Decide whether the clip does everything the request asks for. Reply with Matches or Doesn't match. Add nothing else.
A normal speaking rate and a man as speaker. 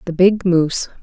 Doesn't match